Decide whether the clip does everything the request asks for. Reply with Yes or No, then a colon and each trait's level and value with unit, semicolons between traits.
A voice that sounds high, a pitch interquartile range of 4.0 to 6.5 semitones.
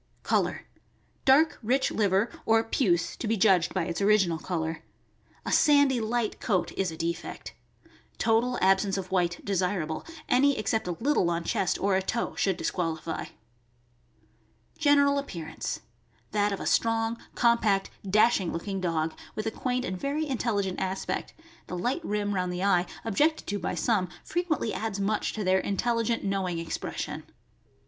Yes: high, 200 Hz; average, 4.5 semitones